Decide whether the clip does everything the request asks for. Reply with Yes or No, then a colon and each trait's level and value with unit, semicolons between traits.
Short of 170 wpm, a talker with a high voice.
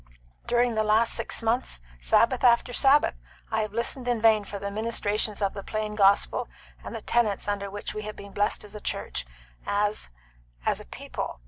No: average, 190 wpm; high, 215 Hz